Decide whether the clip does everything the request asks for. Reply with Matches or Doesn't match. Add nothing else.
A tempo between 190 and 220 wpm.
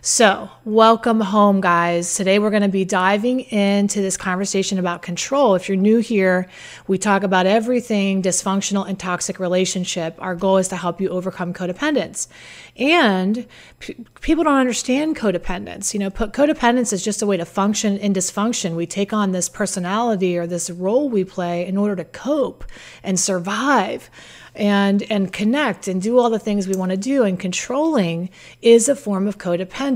Doesn't match